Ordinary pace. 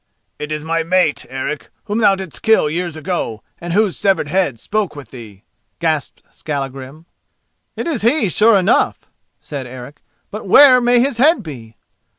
Yes: average, 160 wpm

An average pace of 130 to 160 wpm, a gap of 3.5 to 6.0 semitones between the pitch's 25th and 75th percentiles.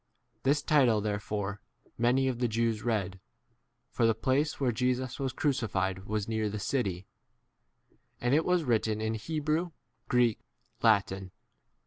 Yes: average, 145 wpm; average, 3.9 semitones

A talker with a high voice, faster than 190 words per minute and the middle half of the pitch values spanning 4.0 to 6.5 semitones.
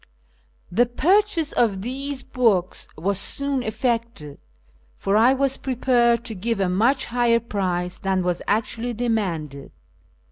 No: high, 230 Hz; slow, 135 wpm; average, 4.8 semitones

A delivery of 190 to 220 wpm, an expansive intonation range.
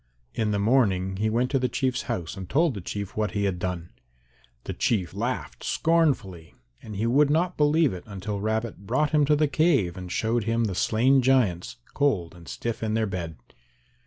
Yes: average, 195 wpm; wide, 5.9 semitones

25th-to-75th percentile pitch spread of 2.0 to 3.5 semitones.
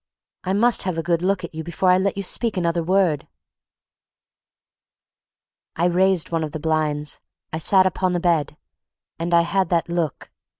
Yes: narrow, 2.5 semitones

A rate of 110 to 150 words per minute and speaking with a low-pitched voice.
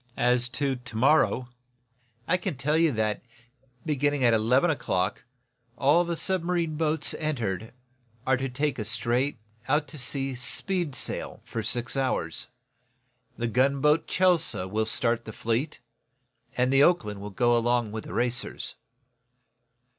Yes: average, 140 wpm; low, 130 Hz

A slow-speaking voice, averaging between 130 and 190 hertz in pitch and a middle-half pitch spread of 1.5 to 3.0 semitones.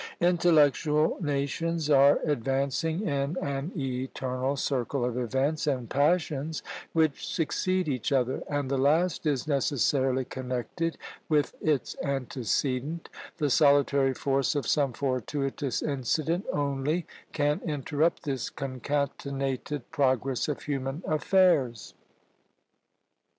Yes: slow, 105 wpm; medium, 140 Hz; narrow, 2.5 semitones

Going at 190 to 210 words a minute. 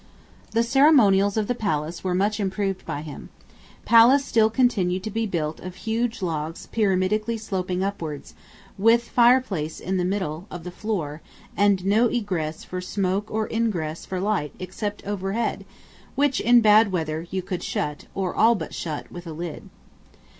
No: average, 165 wpm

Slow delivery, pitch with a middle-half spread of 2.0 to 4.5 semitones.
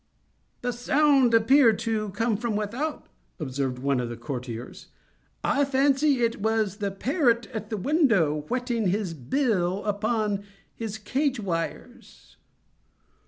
No: slow, 125 wpm; average, 4.9 semitones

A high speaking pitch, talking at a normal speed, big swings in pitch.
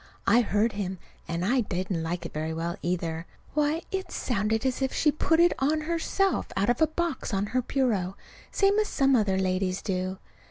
Yes: high, 215 Hz; average, 195 wpm; wide, 8.2 semitones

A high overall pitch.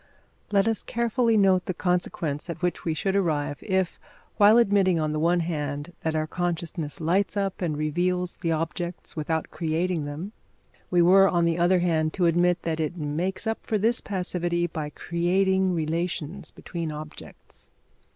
No: medium, 175 Hz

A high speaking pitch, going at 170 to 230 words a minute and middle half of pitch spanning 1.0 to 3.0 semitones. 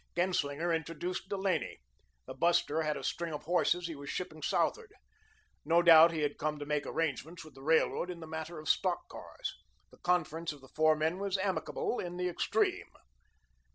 No: medium, 165 Hz; average, 185 wpm; narrow, 2.5 semitones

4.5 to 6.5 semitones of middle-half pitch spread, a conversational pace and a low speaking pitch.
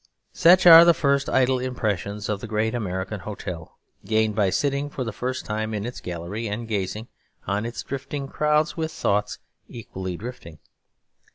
Yes: average, 4.8 semitones; average, 165 wpm; low, 110 Hz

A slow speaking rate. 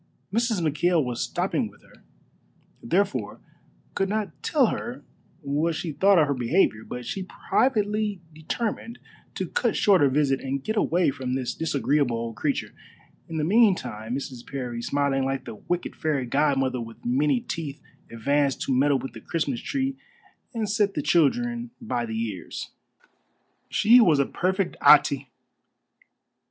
No: average, 150 wpm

